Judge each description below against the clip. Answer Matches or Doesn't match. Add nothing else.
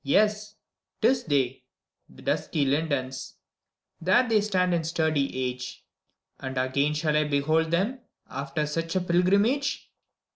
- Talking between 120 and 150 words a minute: Matches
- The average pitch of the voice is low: Doesn't match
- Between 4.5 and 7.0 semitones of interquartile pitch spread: Matches